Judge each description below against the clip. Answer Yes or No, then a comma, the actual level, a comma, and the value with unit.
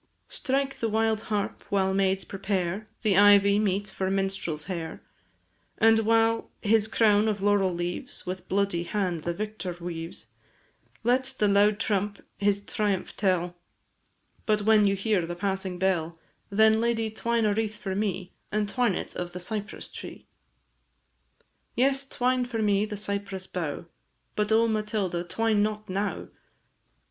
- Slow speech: No, average, 150 wpm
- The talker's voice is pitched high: Yes, high, 205 Hz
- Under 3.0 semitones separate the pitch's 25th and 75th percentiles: Yes, narrow, 2.5 semitones